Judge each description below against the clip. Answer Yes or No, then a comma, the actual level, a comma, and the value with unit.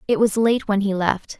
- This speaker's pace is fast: Yes, fast, 260 wpm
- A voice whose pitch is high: Yes, high, 205 Hz